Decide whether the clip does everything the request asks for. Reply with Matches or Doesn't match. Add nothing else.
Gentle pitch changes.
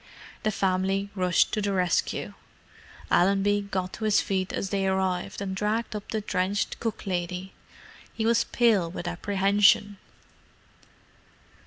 Matches